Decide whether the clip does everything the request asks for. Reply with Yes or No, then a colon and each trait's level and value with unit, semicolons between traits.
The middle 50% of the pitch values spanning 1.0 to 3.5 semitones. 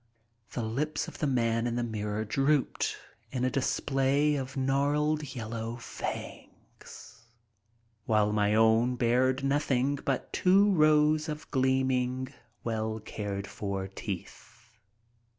No: average, 4.0 semitones